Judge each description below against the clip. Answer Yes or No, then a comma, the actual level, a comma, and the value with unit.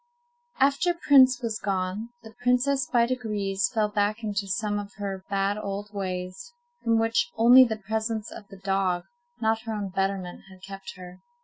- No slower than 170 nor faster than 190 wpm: Yes, average, 175 wpm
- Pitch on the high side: Yes, high, 210 Hz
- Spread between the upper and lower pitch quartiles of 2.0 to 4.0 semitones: Yes, average, 3.0 semitones